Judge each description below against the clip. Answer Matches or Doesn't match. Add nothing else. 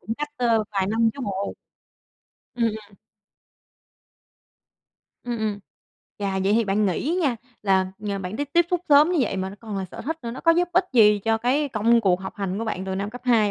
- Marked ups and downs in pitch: Doesn't match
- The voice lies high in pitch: Matches